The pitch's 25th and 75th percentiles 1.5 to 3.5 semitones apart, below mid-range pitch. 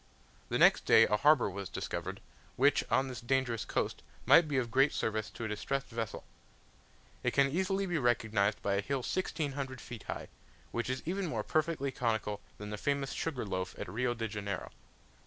No: average, 4.7 semitones; low, 125 Hz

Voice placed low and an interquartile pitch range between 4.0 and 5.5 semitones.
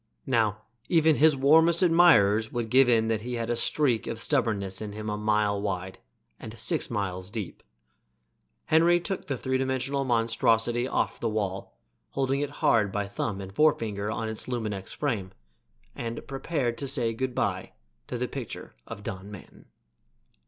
Yes: low, 115 Hz; average, 4.4 semitones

